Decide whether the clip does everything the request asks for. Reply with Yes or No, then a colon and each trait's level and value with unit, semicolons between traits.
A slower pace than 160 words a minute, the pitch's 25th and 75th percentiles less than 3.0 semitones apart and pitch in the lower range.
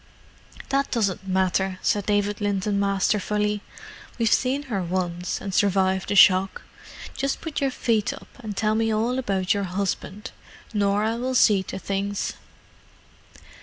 No: slow, 135 wpm; narrow, 2.5 semitones; high, 205 Hz